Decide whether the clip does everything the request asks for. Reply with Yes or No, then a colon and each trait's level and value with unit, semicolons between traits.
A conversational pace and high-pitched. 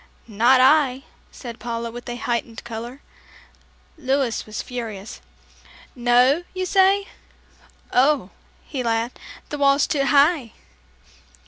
No: slow, 110 wpm; very high, 250 Hz